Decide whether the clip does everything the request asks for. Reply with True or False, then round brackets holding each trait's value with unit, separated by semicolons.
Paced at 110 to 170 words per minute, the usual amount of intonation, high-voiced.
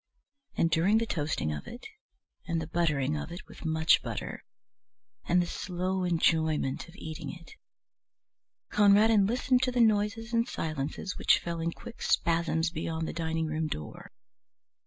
False (155 wpm; 4.1 semitones; 170 Hz)